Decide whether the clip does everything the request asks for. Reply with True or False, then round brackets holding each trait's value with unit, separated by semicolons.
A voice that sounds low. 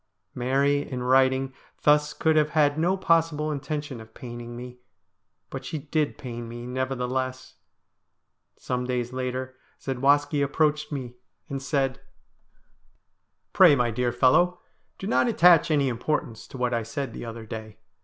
True (130 Hz)